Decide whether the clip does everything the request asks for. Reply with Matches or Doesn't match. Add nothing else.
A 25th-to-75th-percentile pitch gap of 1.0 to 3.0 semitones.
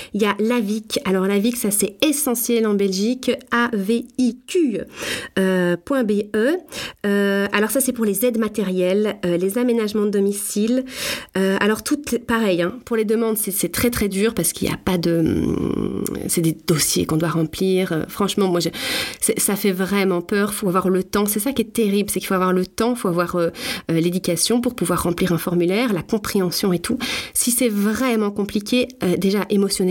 Doesn't match